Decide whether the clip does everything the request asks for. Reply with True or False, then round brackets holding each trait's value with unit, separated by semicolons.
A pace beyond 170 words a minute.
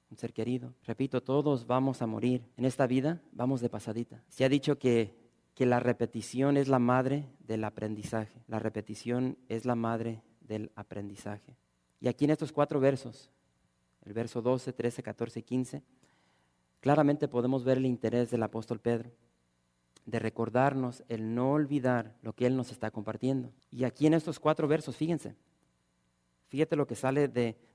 False (165 wpm)